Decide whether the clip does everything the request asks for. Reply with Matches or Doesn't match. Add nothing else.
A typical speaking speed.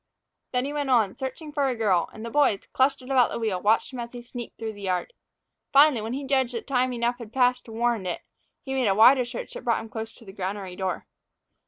Doesn't match